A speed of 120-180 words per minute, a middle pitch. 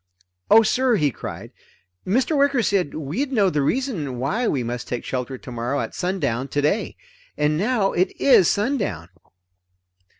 Yes: average, 145 wpm; medium, 180 Hz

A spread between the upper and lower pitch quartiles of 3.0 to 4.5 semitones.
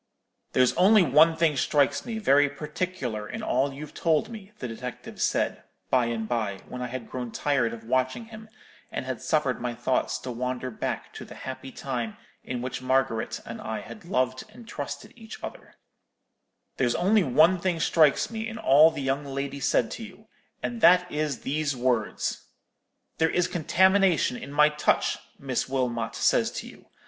No: average, 5.1 semitones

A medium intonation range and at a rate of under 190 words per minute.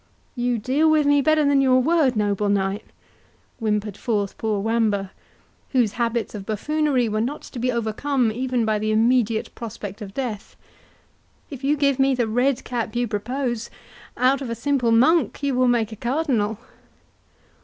Yes: average, 3.8 semitones; average, 165 wpm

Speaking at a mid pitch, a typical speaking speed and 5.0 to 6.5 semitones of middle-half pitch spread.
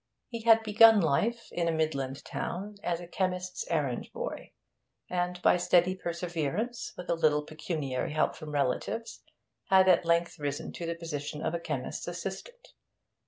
No: medium, 170 Hz; average, 155 wpm; average, 3.6 semitones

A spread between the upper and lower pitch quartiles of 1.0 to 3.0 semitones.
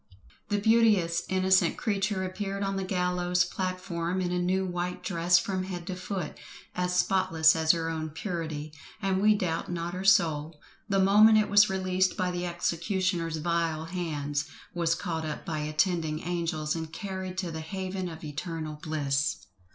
Yes: narrow, 2.5 semitones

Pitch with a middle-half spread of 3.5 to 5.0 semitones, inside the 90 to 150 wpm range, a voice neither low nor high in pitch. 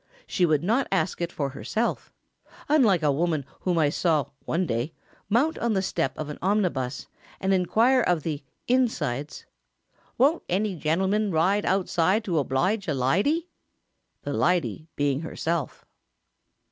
No: wide, 5.6 semitones; average, 145 wpm; medium, 175 Hz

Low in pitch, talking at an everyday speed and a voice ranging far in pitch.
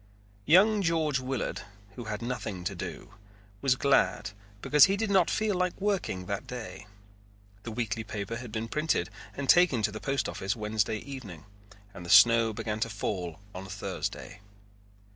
Yes: low, 115 Hz; average, 160 wpm; wide, 6.2 semitones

